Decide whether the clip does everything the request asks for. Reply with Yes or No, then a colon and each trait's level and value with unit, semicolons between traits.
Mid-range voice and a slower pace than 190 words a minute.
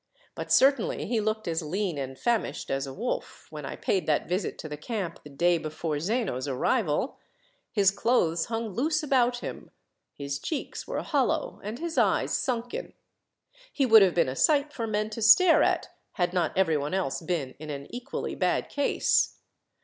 No: high, 195 Hz; average, 180 wpm